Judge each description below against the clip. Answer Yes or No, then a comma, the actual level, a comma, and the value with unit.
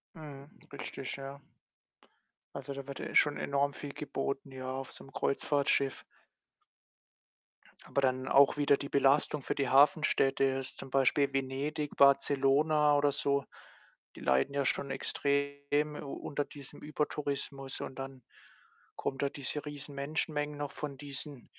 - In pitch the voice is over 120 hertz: Yes, medium, 140 Hz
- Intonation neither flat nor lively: No, narrow, 1.2 semitones